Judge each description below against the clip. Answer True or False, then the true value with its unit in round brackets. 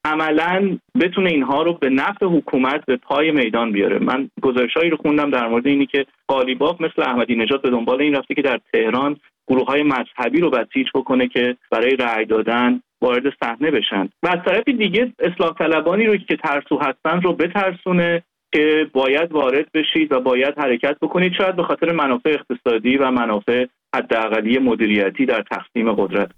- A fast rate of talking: True (170 wpm)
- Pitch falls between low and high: True (145 Hz)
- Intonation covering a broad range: False (4.6 semitones)